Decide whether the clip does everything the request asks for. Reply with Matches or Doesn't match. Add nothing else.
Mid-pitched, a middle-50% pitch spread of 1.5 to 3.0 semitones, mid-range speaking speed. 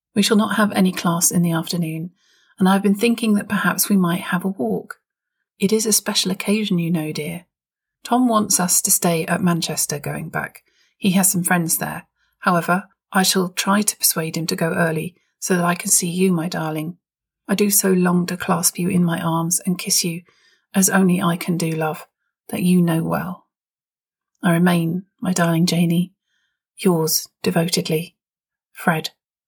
Matches